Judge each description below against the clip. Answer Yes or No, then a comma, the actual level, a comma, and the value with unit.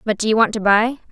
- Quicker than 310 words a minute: Yes, fast, 325 wpm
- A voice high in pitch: Yes, high, 220 Hz